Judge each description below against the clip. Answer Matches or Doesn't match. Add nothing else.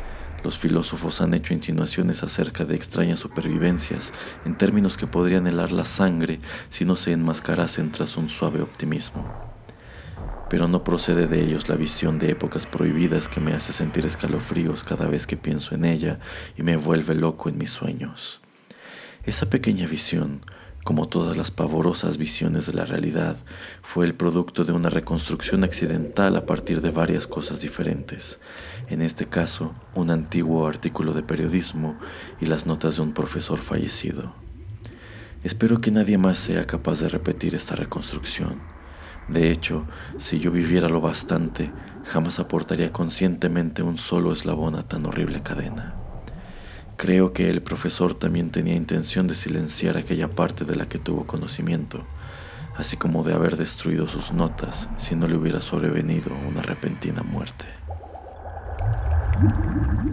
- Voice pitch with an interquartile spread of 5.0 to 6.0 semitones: Doesn't match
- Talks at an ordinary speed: Matches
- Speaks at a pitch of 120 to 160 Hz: Doesn't match